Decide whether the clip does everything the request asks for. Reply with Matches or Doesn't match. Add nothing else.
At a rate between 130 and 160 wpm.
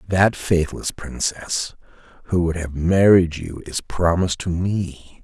Matches